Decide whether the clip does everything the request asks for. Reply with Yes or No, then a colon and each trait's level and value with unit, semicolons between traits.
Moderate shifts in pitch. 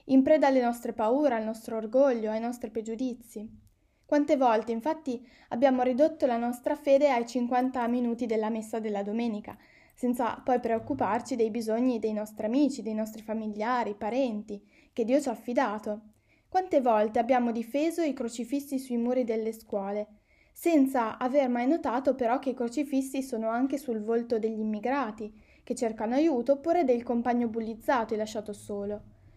Yes: average, 3.2 semitones